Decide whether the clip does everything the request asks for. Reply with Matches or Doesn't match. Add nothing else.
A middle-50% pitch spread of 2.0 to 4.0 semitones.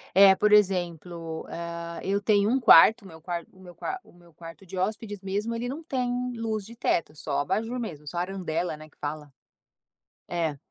Doesn't match